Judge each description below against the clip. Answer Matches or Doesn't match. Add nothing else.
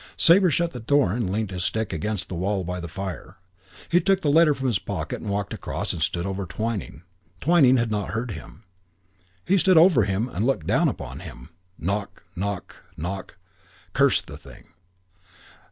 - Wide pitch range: Matches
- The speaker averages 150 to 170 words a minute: Doesn't match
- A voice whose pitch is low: Matches